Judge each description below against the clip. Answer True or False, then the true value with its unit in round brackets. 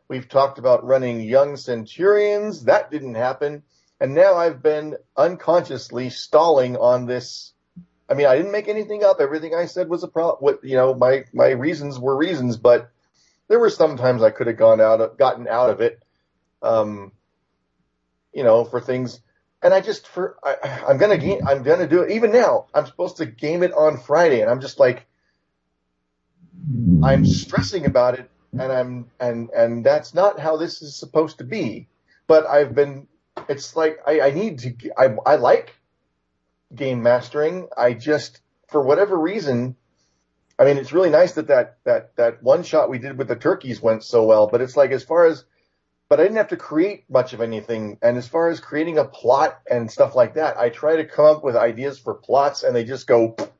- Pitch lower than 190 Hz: True (135 Hz)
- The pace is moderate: True (195 wpm)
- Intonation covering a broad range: True (5.7 semitones)